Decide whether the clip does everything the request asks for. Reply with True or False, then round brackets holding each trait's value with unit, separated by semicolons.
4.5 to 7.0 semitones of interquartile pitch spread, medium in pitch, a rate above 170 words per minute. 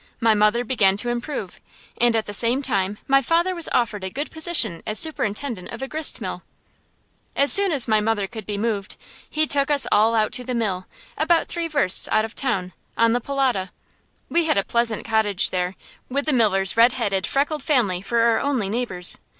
False (5.1 semitones; 230 Hz; 200 wpm)